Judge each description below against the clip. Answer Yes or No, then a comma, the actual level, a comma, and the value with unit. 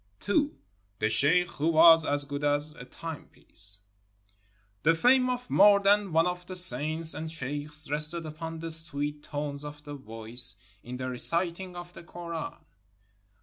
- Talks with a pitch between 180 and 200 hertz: No, medium, 155 Hz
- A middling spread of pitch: Yes, average, 3.2 semitones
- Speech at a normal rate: Yes, average, 155 wpm